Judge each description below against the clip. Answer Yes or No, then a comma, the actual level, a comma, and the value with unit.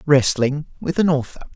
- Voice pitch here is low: No, medium, 145 Hz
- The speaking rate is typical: Yes, average, 155 wpm